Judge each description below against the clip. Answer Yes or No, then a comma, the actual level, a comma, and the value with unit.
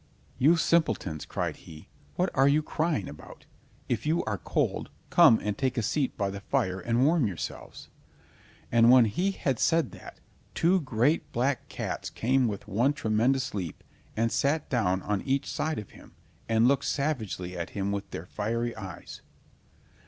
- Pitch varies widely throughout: Yes, wide, 5.7 semitones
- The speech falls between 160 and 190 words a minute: Yes, average, 165 wpm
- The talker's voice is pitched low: Yes, low, 120 Hz